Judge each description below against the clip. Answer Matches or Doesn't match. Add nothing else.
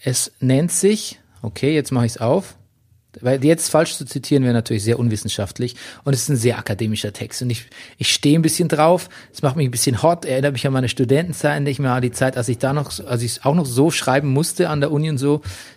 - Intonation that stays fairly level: Doesn't match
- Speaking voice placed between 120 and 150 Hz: Matches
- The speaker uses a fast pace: Matches